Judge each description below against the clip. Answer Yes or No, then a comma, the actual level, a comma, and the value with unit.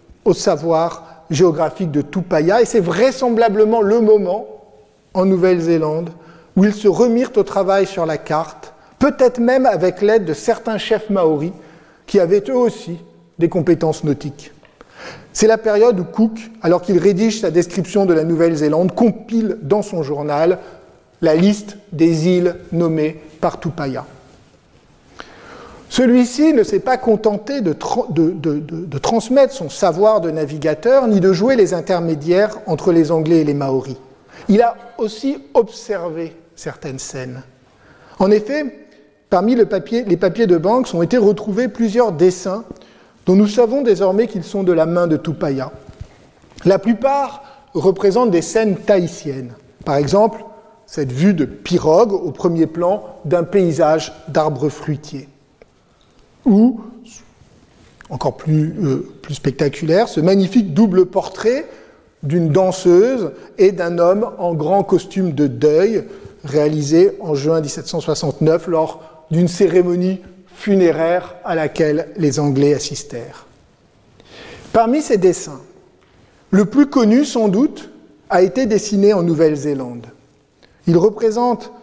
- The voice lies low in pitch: No, medium, 180 Hz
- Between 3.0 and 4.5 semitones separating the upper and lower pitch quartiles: No, wide, 5.6 semitones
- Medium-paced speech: No, slow, 135 wpm